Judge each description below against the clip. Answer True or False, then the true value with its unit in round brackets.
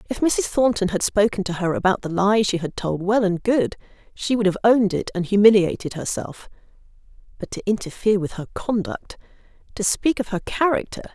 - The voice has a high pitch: True (200 Hz)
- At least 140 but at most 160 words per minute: False (180 wpm)